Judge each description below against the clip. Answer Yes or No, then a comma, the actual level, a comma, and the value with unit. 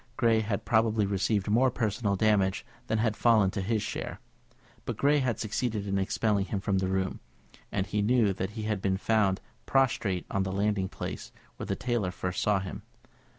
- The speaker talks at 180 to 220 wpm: Yes, average, 190 wpm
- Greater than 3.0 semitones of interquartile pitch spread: No, narrow, 2.5 semitones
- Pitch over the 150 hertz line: No, low, 105 Hz